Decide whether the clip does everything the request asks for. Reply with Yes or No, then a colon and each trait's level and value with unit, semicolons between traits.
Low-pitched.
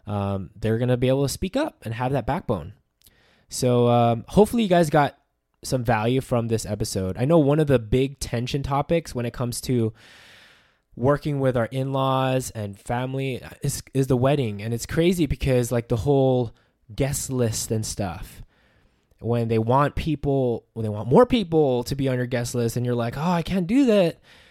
Yes: low, 125 Hz